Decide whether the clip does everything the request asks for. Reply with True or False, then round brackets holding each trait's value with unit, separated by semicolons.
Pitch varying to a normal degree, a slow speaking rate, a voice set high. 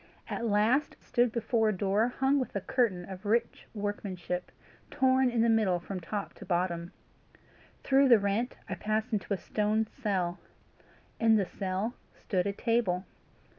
False (3.8 semitones; 165 wpm; 210 Hz)